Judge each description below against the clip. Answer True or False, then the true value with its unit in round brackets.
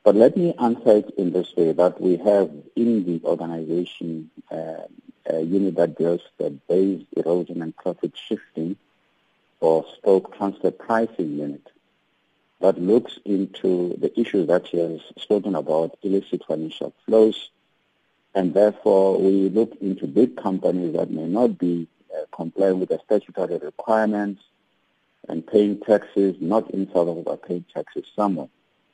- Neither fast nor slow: True (145 wpm)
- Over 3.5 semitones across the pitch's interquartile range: False (3.2 semitones)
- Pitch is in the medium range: False (95 Hz)